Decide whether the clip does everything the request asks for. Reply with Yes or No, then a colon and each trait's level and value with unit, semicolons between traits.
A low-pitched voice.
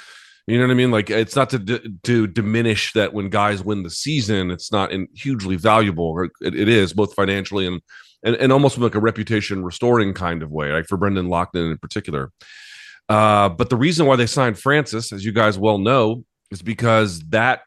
Yes: low, 105 Hz